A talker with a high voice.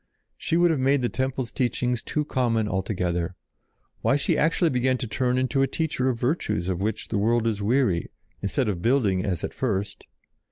No: low, 120 Hz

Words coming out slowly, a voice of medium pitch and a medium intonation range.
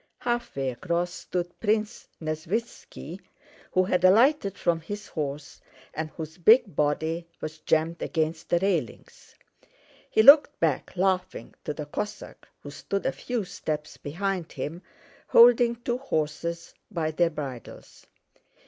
Yes: slow, 130 wpm; medium, 175 Hz; average, 4.7 semitones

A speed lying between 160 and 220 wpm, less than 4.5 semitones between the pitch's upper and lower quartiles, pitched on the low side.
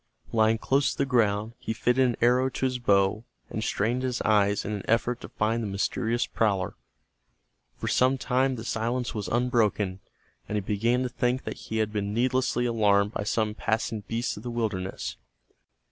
Yes: average, 185 wpm; average, 2.8 semitones; low, 115 Hz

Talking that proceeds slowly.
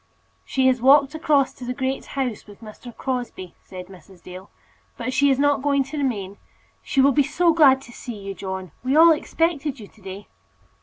No: average, 200 wpm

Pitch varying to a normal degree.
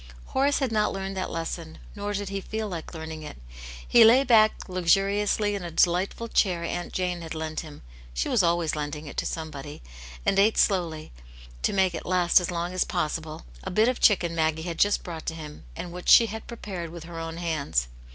Yes: average, 3.8 semitones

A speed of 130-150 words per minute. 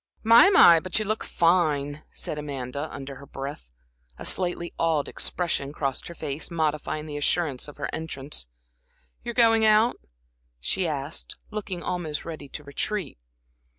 Yes: average, 145 wpm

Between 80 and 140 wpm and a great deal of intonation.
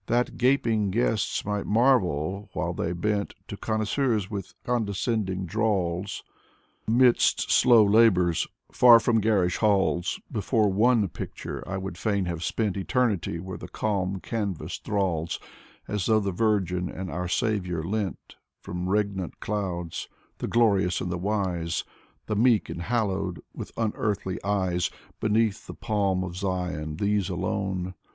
No: slow, 135 wpm; average, 3.2 semitones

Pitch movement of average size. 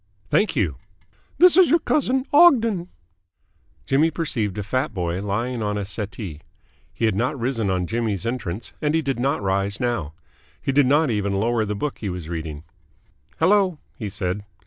No: wide, 7.1 semitones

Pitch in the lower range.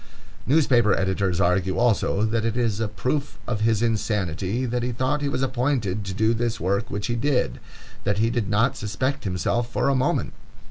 Yes: low, 115 Hz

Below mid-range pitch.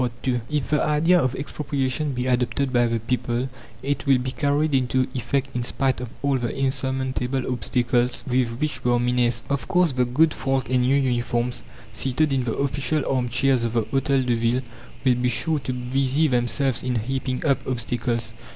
Yes: low, 130 Hz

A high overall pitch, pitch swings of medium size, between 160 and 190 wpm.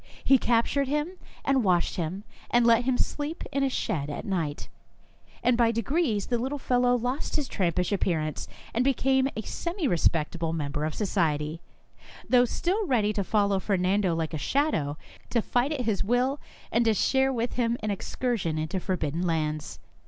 No: high, 225 Hz; wide, 7.1 semitones; average, 175 wpm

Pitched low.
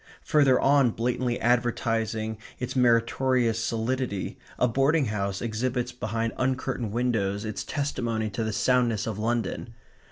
Yes: low, 120 Hz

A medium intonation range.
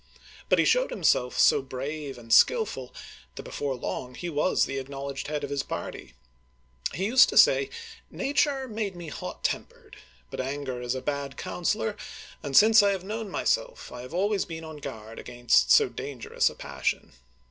No: wide, 8.0 semitones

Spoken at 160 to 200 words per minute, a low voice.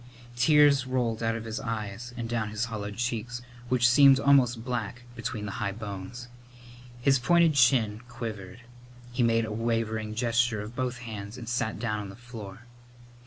Yes: average, 165 wpm; low, 115 Hz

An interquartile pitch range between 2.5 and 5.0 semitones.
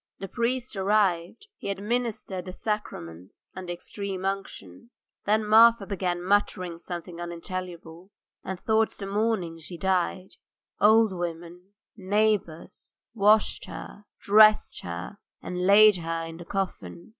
Yes: average, 3.5 semitones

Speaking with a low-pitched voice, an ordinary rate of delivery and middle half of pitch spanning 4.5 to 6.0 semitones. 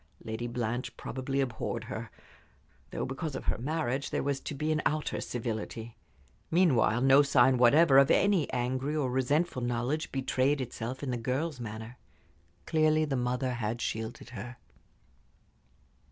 No: low, 130 Hz; average, 145 wpm; average, 3.2 semitones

